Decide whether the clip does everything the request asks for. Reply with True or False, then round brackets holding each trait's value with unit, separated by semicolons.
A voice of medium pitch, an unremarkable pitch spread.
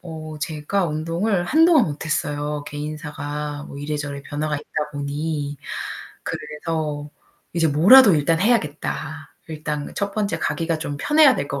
False (155 Hz; 2.3 semitones)